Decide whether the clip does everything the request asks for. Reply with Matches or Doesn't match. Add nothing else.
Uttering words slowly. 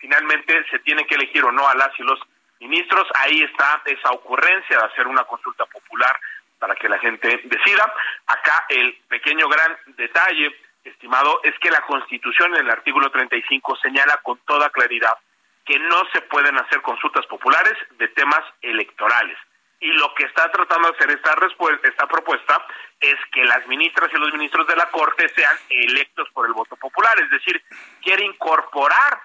Doesn't match